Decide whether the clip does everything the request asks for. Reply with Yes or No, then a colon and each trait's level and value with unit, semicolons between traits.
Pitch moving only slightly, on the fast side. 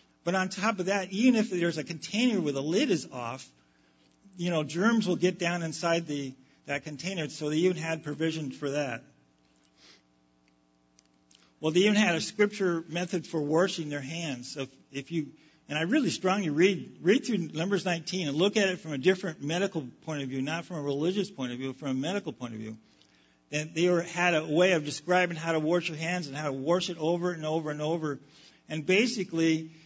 No: average, 4.3 semitones; fast, 215 wpm